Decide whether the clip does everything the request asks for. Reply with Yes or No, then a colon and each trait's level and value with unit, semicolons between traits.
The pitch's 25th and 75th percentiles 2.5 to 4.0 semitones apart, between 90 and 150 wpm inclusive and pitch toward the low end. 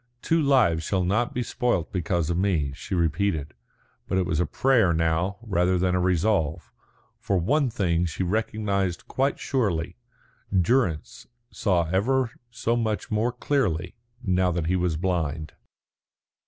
No: average, 4.8 semitones; average, 145 wpm; very low, 95 Hz